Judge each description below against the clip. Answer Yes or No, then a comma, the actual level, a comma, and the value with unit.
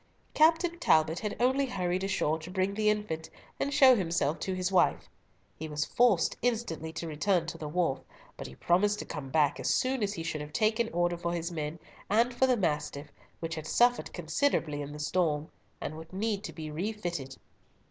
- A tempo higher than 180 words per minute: Yes, average, 200 wpm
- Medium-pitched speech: Yes, medium, 175 Hz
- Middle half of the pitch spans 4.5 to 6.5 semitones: Yes, wide, 5.4 semitones